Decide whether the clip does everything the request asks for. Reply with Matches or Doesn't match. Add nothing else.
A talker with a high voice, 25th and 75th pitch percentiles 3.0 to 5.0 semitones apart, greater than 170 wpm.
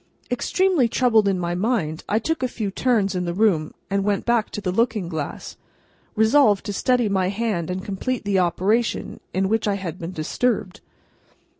Matches